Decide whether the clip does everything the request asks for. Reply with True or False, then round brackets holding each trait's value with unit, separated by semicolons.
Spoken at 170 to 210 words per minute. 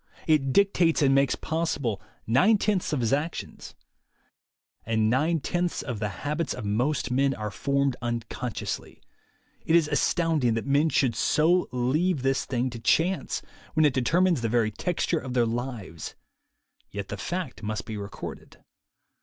False (155 wpm)